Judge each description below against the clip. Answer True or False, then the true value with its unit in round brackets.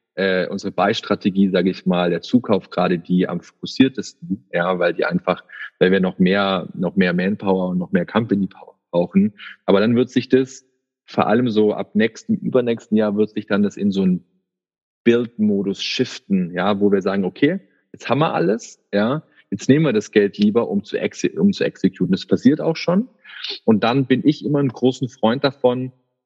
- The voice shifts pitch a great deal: True (6.2 semitones)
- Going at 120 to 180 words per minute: False (190 wpm)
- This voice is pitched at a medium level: False (110 Hz)